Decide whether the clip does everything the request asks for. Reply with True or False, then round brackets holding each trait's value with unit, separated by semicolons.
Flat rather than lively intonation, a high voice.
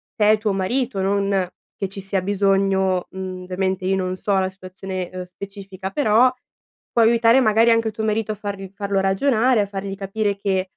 True (2.2 semitones; 195 Hz)